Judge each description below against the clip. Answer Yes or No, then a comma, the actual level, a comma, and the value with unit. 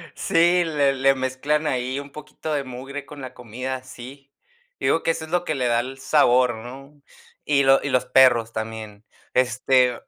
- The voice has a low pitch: Yes, low, 130 Hz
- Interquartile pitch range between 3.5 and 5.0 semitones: No, narrow, 2.4 semitones